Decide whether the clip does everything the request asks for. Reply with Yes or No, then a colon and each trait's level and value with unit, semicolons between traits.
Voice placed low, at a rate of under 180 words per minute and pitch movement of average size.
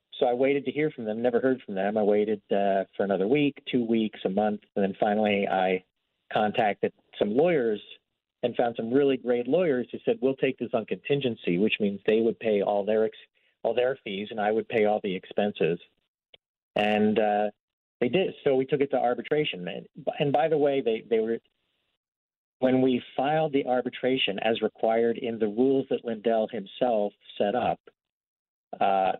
No: low, 115 Hz; average, 190 wpm; average, 3.9 semitones